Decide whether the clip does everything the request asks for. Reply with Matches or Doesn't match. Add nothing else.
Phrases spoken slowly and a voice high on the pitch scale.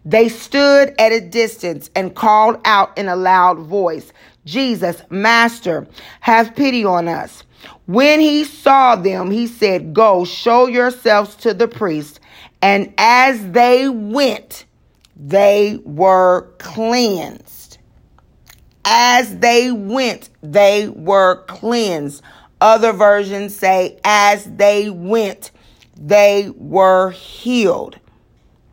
Matches